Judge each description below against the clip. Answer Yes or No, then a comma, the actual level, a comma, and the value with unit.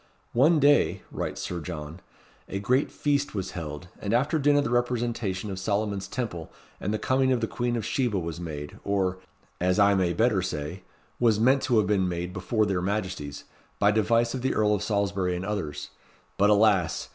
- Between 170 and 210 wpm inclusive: Yes, average, 190 wpm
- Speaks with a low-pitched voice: Yes, low, 100 Hz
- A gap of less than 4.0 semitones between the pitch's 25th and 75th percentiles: No, average, 4.7 semitones